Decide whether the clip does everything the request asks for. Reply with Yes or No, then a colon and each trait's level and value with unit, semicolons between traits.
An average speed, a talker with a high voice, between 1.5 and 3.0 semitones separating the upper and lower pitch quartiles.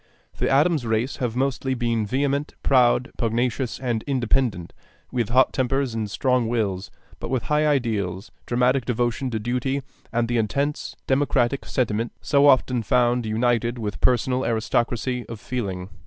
No: average, 145 wpm; low, 120 Hz; narrow, 2.5 semitones